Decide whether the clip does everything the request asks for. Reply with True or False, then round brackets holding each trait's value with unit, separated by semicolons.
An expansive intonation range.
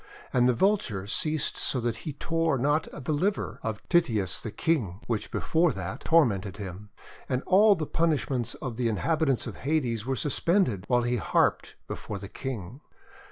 True (6.9 semitones)